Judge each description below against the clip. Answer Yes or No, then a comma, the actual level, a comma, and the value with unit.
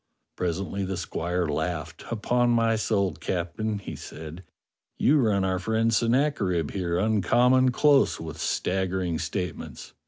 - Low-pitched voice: Yes, very low, 95 Hz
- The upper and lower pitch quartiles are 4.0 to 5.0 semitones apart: Yes, average, 4.6 semitones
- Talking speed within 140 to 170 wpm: Yes, average, 145 wpm